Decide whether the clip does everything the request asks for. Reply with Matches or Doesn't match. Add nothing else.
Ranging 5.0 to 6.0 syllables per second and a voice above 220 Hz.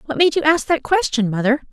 Matches